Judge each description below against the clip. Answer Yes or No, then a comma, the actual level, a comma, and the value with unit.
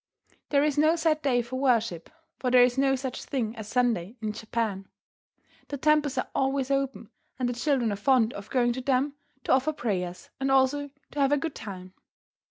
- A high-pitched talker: Yes, very high, 255 Hz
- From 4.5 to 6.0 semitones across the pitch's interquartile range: No, average, 3.6 semitones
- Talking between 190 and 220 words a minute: Yes, average, 195 wpm